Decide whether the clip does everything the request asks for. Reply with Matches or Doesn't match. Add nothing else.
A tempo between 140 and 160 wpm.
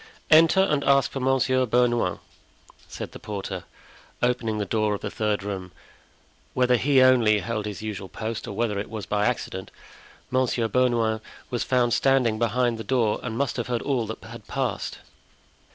Doesn't match